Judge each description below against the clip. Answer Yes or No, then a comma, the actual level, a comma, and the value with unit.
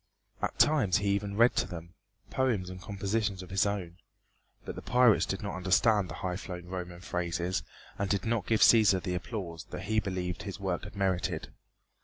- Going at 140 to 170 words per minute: No, average, 185 wpm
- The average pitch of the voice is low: Yes, very low, 95 Hz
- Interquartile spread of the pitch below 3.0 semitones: Yes, narrow, 2.5 semitones